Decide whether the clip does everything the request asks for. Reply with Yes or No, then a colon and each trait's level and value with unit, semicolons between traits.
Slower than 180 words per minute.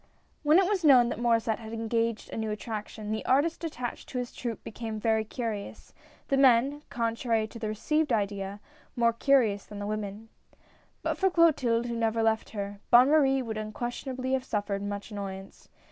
No: average, 190 wpm